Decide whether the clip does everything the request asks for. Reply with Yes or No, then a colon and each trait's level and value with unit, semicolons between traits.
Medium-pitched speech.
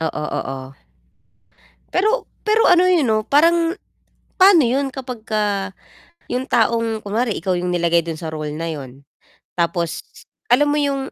No: high, 230 Hz